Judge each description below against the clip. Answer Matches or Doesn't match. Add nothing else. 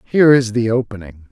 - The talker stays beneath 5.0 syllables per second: Doesn't match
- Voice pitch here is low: Matches